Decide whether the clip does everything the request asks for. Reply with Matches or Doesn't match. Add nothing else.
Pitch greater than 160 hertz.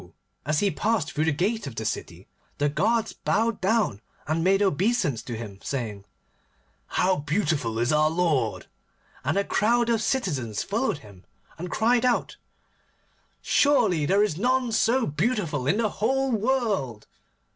Matches